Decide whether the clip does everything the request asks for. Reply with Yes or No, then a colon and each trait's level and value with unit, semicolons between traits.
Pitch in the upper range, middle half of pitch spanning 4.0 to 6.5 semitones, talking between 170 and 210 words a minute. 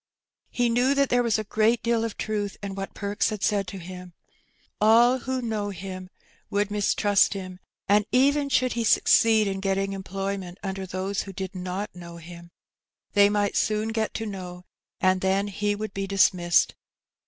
No: high, 200 Hz; narrow, 2.5 semitones; average, 180 wpm